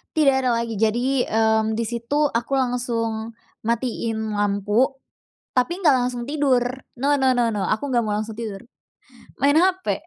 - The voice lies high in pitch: Yes, high, 240 Hz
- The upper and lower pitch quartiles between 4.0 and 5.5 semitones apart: No, average, 3.6 semitones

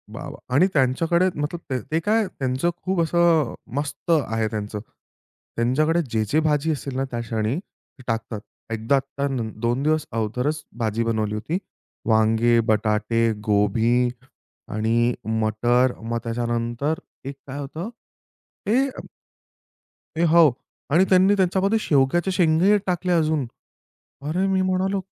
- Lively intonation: Yes, wide, 6.7 semitones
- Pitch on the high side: No, low, 135 Hz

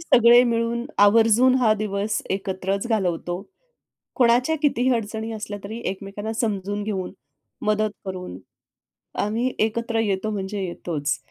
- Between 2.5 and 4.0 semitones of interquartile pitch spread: Yes, average, 2.9 semitones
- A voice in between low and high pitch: No, high, 215 Hz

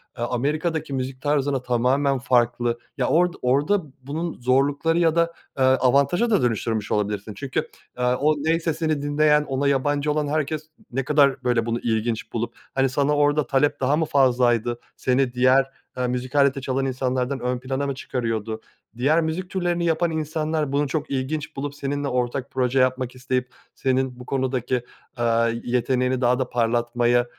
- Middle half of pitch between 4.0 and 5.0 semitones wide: No, average, 3.0 semitones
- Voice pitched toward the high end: No, low, 135 Hz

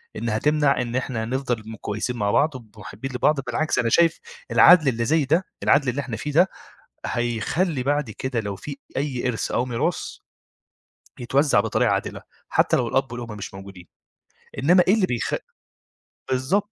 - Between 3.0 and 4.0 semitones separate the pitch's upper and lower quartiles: No, average, 4.5 semitones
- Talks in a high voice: No, low, 130 Hz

